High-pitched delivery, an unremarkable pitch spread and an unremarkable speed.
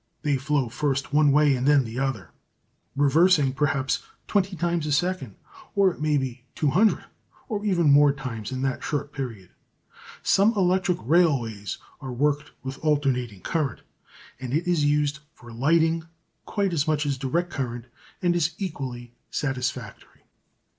No: medium, 145 Hz; average, 4.0 semitones; average, 155 wpm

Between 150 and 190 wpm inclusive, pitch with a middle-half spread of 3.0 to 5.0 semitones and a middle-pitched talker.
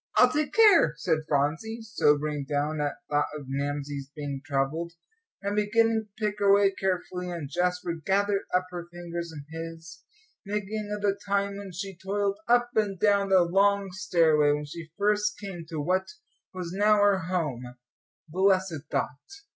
Yes: average, 165 wpm; average, 4.4 semitones; medium, 180 Hz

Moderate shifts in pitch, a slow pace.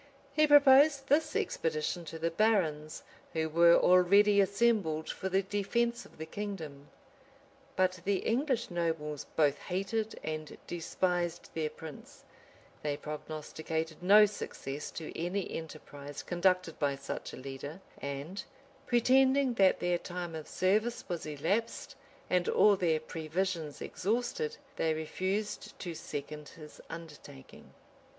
Yes: average, 4.9 semitones; slow, 130 wpm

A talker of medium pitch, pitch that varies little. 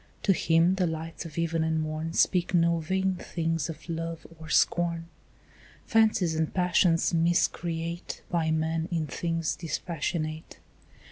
Yes: medium, 165 Hz; narrow, 1.2 semitones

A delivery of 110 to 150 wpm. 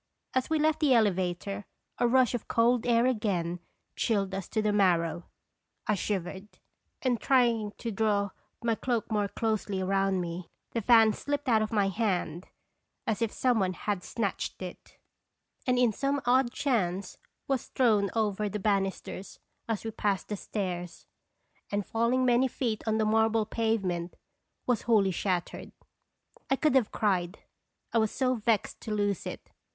No: average, 160 wpm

